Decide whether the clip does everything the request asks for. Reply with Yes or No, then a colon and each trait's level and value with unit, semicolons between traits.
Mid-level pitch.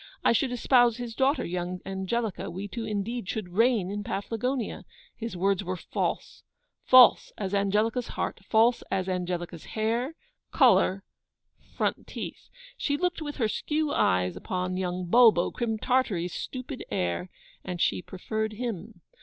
No: high, 215 Hz